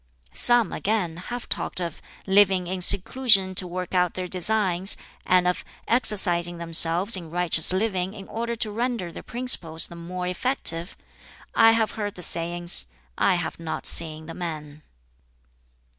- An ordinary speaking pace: Yes, average, 150 wpm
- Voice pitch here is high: No, medium, 180 Hz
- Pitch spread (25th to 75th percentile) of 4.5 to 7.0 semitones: No, average, 3.5 semitones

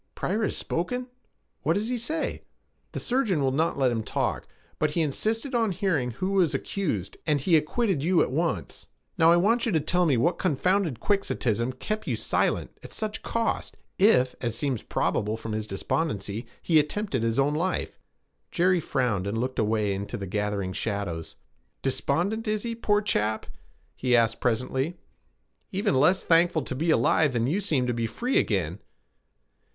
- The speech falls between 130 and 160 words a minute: No, average, 175 wpm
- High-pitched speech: No, medium, 150 Hz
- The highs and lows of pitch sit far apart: Yes, wide, 8.7 semitones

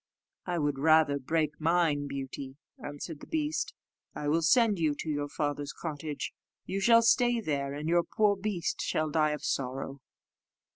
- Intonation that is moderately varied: Yes, average, 3.5 semitones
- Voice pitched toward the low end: No, medium, 155 Hz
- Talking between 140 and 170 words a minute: Yes, average, 160 wpm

